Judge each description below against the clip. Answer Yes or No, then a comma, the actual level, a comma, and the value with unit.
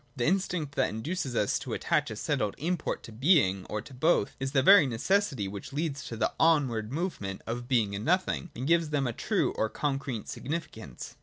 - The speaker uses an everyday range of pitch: No, wide, 6.5 semitones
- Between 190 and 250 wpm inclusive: Yes, average, 200 wpm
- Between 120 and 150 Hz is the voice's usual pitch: Yes, low, 135 Hz